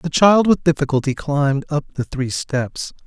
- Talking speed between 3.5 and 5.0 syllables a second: Yes, 4.7 syllables/s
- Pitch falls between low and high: Yes, medium, 145 Hz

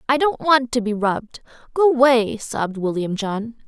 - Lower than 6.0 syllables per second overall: Yes, 4.2 syllables/s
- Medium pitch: No, high, 240 Hz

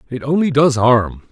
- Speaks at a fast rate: No, average, 185 wpm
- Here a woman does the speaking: No, male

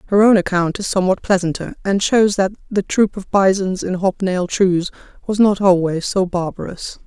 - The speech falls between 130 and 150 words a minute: No, average, 185 wpm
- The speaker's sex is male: No, female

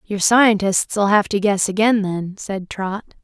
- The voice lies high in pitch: Yes, high, 205 Hz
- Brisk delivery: No, average, 165 wpm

